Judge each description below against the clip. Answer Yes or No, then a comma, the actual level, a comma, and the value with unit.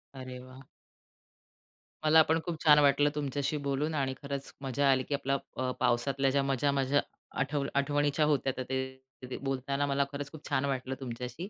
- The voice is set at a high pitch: No, medium, 140 Hz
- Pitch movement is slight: Yes, narrow, 1.6 semitones